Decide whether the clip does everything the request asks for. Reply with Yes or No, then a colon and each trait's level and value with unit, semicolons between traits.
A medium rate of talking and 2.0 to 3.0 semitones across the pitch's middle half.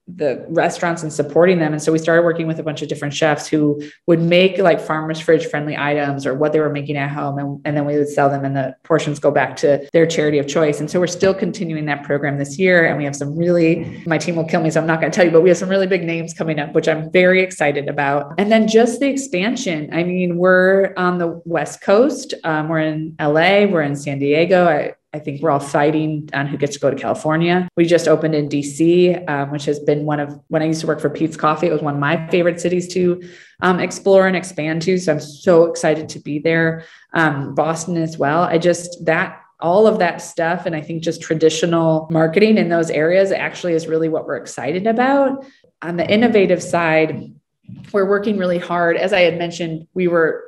No: fast, 240 wpm; average, 2.7 semitones